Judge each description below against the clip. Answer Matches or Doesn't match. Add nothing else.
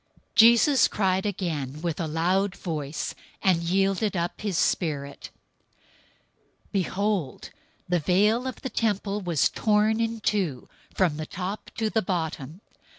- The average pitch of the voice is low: Doesn't match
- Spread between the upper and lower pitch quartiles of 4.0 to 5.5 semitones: Matches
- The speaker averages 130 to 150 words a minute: Matches